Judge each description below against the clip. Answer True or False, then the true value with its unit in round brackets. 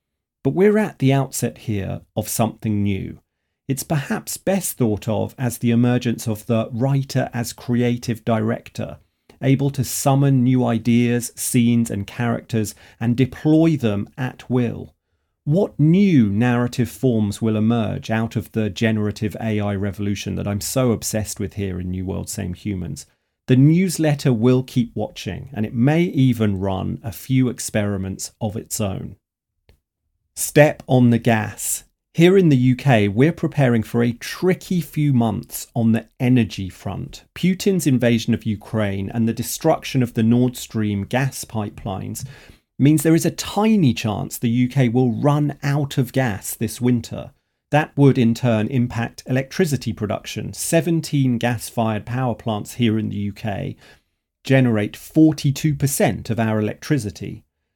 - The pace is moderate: True (150 wpm)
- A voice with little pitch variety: False (3.9 semitones)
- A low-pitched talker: True (120 Hz)